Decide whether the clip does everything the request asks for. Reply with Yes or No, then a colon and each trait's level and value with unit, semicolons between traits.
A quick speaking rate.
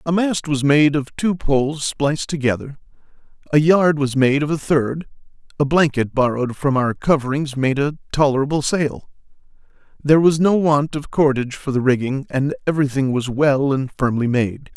No: average, 170 wpm